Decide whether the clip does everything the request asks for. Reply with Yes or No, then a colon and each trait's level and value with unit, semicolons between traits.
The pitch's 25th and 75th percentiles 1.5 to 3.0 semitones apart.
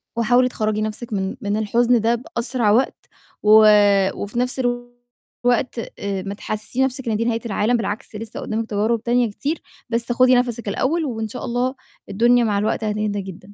Yes: narrow, 2.5 semitones